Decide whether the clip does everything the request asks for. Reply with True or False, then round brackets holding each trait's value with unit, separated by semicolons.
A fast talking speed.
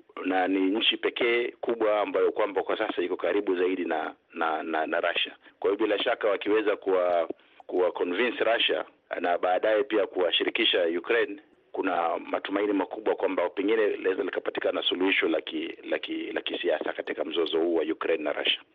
True (150 wpm)